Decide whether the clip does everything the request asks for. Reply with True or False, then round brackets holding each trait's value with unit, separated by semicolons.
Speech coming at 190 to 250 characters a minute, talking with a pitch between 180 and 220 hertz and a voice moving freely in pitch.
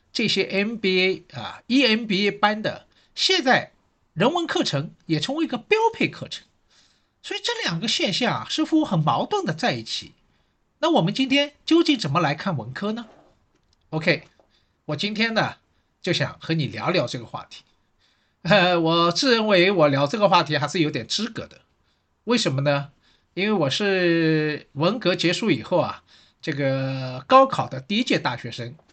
True (245 characters per minute; 185 Hz; 7.9 semitones)